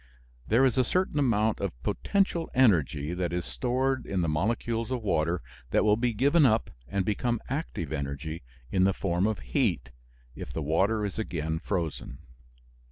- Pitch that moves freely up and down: Yes, wide, 6.8 semitones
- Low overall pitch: Yes, low, 100 Hz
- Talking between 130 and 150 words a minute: No, average, 165 wpm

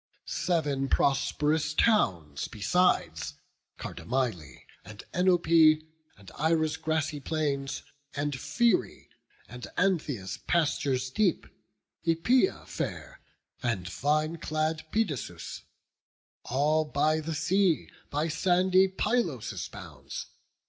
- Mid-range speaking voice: Yes, medium, 155 Hz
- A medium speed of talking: No, slow, 90 wpm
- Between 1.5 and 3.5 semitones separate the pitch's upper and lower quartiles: No, average, 4.0 semitones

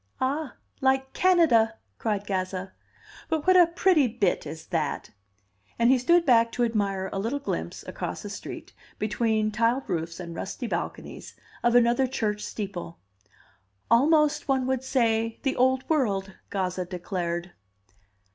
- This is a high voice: Yes, high, 230 Hz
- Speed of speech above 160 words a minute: No, average, 140 wpm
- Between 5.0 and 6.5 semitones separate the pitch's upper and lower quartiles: Yes, wide, 5.5 semitones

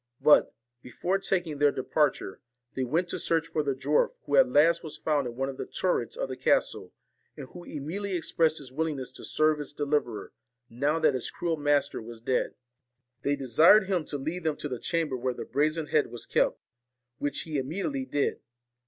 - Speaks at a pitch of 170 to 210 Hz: No, medium, 150 Hz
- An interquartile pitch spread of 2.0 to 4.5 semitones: Yes, average, 3.4 semitones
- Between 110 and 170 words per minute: No, average, 195 wpm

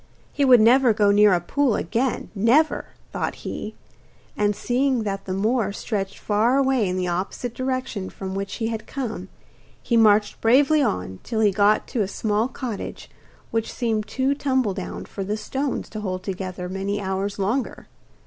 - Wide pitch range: No, average, 4.2 semitones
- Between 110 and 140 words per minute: No, average, 170 wpm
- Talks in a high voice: Yes, high, 215 Hz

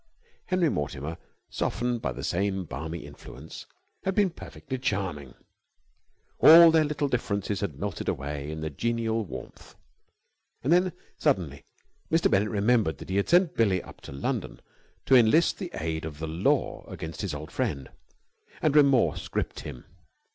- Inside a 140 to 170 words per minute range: Yes, average, 155 wpm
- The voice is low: Yes, low, 100 Hz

